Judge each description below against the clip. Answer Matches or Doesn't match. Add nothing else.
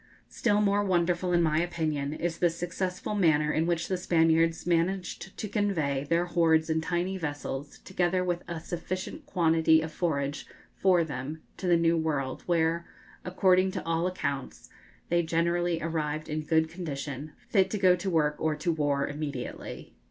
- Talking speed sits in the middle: Matches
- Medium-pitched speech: Matches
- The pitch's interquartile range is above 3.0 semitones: Doesn't match